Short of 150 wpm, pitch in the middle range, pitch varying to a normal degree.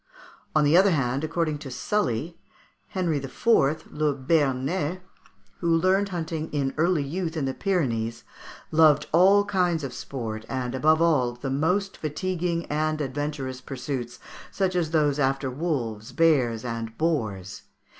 Yes: average, 140 wpm; medium, 150 Hz; average, 4.4 semitones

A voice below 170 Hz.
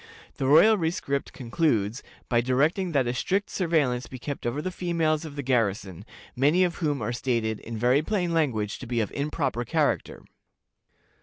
Yes: medium, 140 Hz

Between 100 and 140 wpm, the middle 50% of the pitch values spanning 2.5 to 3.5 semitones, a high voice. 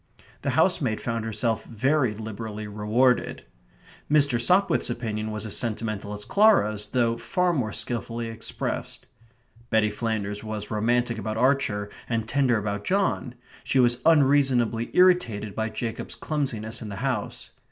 No: slow, 135 wpm; average, 2.8 semitones; low, 115 Hz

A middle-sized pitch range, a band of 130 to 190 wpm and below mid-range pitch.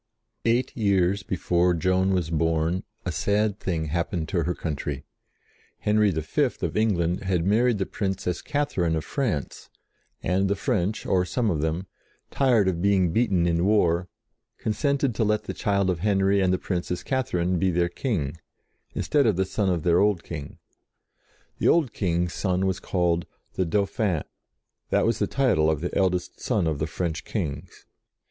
Yes: average, 3.4 semitones; average, 165 wpm; very low, 95 Hz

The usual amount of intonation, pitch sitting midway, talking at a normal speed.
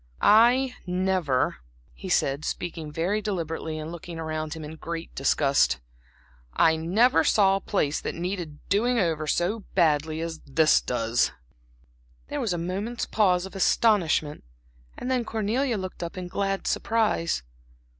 Yes: average, 4.5 semitones; medium, 175 Hz; average, 145 wpm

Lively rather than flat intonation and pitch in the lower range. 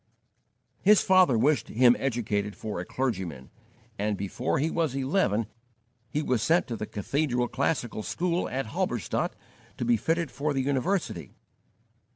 Yes: wide, 6.2 semitones; low, 130 Hz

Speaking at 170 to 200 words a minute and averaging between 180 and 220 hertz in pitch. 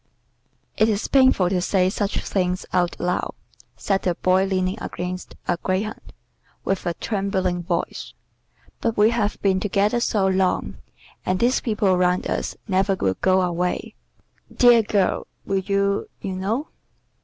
No: average, 145 wpm; high, 190 Hz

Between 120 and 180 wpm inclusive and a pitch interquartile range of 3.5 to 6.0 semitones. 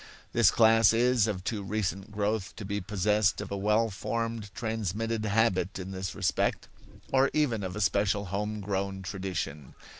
No: average, 160 wpm; narrow, 2.5 semitones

